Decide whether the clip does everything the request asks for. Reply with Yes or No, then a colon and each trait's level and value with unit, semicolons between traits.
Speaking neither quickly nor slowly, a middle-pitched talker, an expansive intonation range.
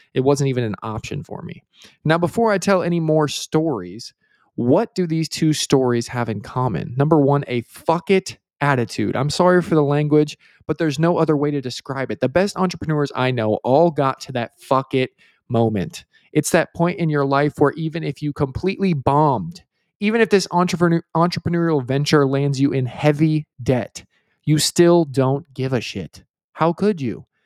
No: average, 185 wpm; medium, 145 Hz; average, 4.2 semitones